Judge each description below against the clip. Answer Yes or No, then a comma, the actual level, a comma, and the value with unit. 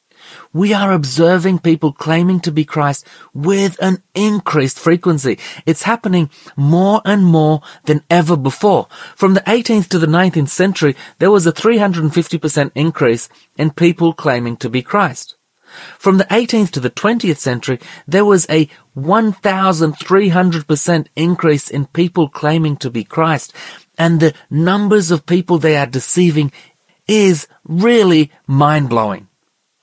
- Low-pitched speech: No, medium, 165 Hz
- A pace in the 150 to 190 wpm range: No, slow, 135 wpm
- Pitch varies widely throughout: No, average, 3.9 semitones